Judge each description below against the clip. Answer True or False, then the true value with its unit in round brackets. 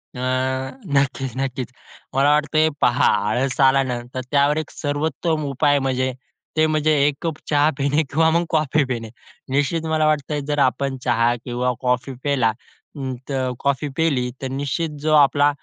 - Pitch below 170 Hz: True (140 Hz)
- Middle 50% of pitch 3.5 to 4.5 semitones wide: False (2.7 semitones)